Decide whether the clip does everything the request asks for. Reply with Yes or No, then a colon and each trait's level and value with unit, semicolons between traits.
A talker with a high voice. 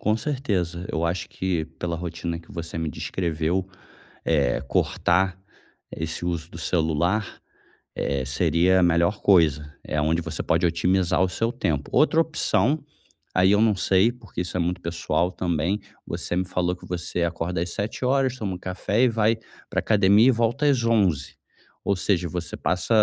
No: very low, 90 Hz